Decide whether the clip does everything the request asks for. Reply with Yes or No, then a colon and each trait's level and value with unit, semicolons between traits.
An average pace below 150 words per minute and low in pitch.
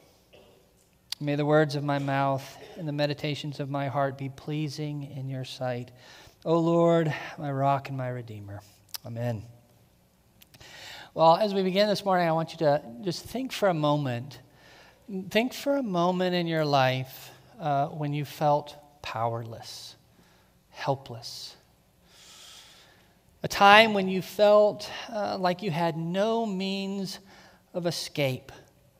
No: slow, 135 wpm; medium, 145 Hz